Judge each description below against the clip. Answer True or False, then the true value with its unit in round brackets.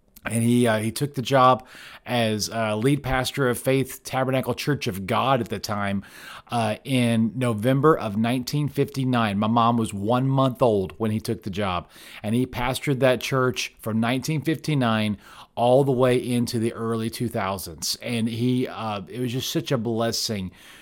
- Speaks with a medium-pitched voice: False (120 Hz)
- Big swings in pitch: False (2.8 semitones)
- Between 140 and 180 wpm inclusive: True (170 wpm)